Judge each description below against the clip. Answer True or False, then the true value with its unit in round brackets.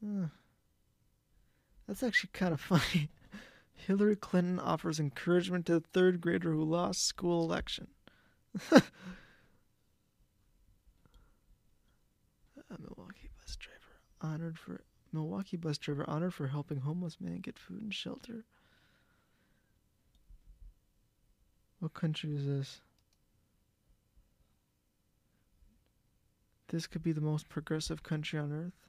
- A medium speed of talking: False (100 wpm)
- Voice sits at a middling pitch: True (160 Hz)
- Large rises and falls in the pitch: False (3.6 semitones)